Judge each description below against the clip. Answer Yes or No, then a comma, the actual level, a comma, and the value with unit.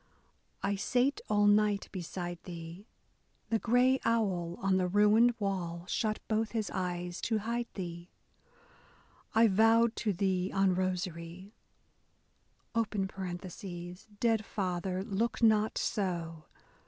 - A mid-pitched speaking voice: No, high, 195 Hz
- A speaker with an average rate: No, slow, 110 wpm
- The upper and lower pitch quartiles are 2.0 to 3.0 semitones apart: No, average, 3.6 semitones